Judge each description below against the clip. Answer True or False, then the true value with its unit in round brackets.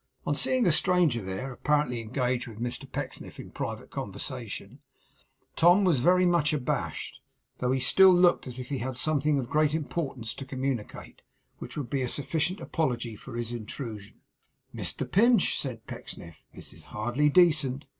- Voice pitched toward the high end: False (135 Hz)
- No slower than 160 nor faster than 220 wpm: True (165 wpm)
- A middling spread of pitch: True (4.8 semitones)